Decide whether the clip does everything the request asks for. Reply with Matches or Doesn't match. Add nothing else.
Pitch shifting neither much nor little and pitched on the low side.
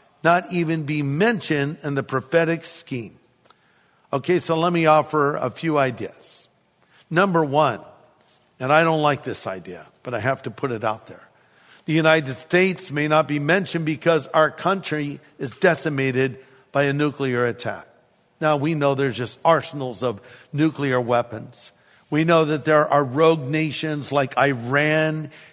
Doesn't match